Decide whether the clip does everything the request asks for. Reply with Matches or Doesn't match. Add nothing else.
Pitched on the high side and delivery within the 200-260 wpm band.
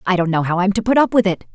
Doesn't match